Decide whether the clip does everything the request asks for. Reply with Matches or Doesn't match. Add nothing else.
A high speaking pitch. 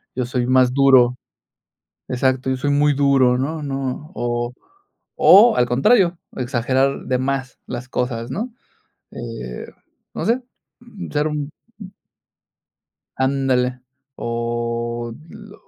Doesn't match